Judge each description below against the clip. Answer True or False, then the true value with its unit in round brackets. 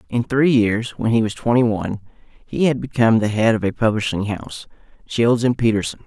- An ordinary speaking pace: True (190 wpm)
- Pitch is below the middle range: True (115 Hz)